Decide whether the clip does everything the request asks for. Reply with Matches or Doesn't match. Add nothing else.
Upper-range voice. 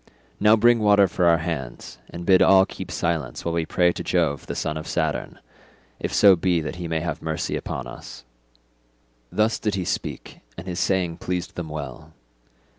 Doesn't match